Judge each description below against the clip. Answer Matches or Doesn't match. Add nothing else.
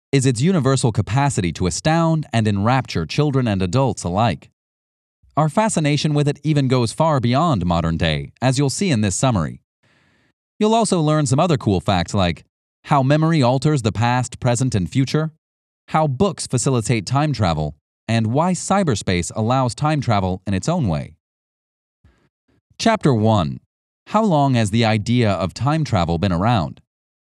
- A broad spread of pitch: Matches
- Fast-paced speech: Doesn't match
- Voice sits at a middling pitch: Doesn't match